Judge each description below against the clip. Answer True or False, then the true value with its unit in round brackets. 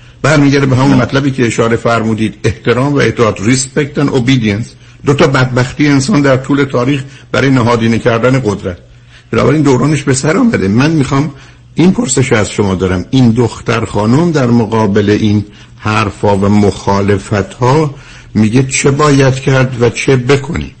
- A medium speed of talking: False (160 wpm)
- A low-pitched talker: True (125 Hz)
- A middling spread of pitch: True (3.6 semitones)